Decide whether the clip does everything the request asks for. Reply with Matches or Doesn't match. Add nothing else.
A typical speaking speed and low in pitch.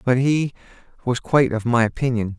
Matches